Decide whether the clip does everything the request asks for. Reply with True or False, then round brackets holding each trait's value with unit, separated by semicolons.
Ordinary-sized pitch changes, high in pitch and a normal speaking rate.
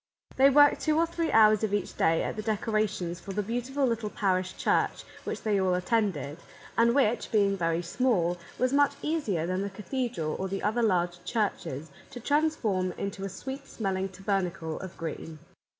True (4.9 semitones; 205 Hz; 180 wpm)